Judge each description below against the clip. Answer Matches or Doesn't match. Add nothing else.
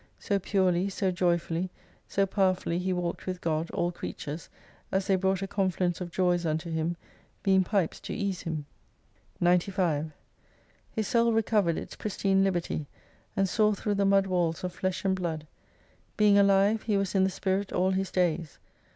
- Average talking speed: Matches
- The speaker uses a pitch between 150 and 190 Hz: Matches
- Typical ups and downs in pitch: Doesn't match